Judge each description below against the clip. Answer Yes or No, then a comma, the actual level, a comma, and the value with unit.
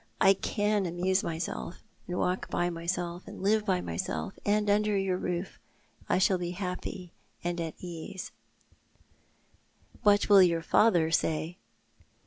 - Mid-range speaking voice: Yes, medium, 180 Hz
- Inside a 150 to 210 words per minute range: No, average, 140 wpm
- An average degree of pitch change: No, narrow, 2.2 semitones